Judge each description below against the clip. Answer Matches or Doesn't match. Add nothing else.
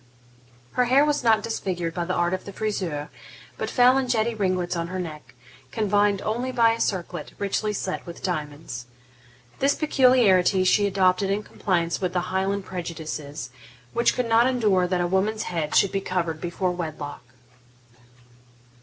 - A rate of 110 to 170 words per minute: Matches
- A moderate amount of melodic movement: Matches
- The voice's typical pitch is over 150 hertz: Matches